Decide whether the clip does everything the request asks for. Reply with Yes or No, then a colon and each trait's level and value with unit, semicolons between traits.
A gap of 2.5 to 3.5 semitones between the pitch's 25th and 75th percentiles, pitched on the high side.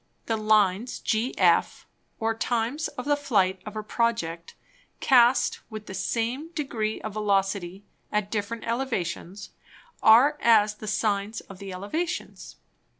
Yes: average, 2.8 semitones; high, 215 Hz